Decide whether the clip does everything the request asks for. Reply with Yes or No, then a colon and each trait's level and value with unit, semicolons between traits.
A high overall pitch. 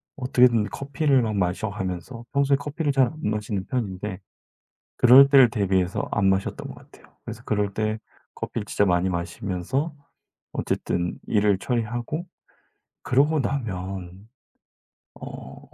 No: low, 110 Hz